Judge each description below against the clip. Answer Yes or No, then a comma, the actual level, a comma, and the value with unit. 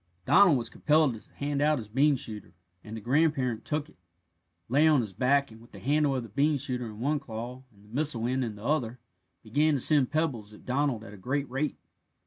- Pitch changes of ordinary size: Yes, average, 4.4 semitones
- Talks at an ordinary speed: No, fast, 225 wpm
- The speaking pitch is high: No, low, 130 Hz